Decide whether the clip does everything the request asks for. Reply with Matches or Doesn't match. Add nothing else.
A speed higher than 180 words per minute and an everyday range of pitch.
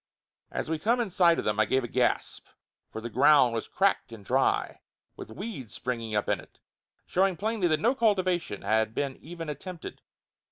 Doesn't match